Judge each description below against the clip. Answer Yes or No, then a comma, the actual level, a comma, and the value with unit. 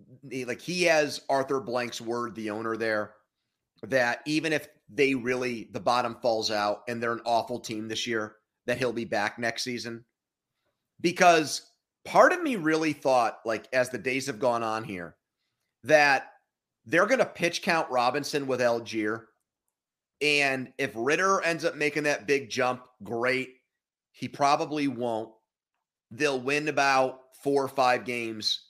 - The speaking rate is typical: Yes, average, 155 wpm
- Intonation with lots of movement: No, average, 3.7 semitones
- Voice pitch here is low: Yes, low, 125 Hz